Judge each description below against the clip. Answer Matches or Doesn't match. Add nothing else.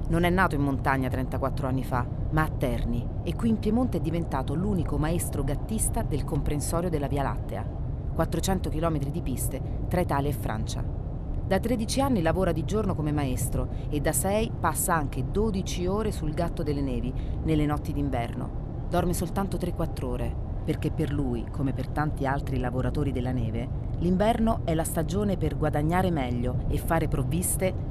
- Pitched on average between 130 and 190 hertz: Matches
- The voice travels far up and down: Doesn't match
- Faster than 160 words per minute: Matches